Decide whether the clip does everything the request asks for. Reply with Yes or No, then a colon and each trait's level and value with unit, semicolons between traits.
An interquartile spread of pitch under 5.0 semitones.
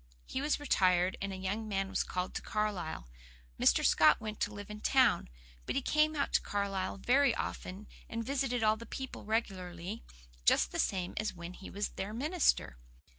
Yes: average, 4.2 semitones